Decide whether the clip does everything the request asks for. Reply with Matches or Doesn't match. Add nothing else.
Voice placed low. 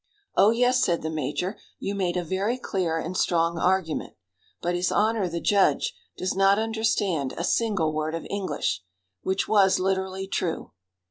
Doesn't match